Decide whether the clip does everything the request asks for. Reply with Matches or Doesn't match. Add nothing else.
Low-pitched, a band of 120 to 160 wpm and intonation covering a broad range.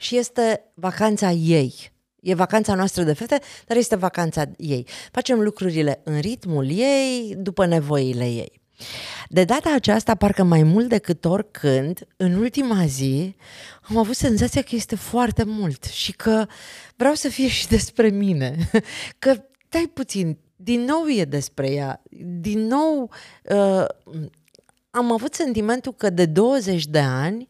Doesn't match